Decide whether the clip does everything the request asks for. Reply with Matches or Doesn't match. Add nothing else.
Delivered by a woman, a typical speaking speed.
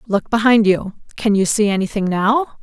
Matches